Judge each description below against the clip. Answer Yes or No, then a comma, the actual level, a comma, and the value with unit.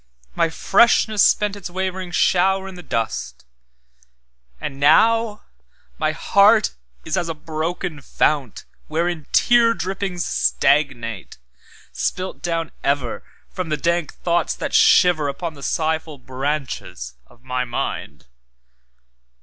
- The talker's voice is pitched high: No, medium, 160 Hz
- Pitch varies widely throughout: Yes, wide, 6.2 semitones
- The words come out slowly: Yes, slow, 105 wpm